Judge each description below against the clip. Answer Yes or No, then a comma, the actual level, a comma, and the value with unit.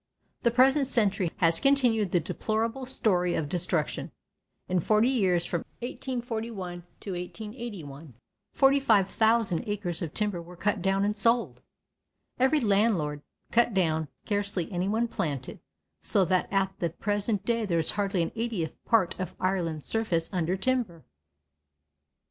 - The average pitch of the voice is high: Yes, high, 200 Hz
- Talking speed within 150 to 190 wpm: No, slow, 135 wpm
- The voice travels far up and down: No, average, 4.7 semitones